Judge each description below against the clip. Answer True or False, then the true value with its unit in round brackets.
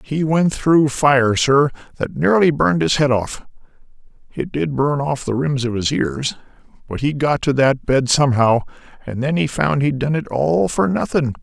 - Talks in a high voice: False (135 Hz)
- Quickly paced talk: False (185 wpm)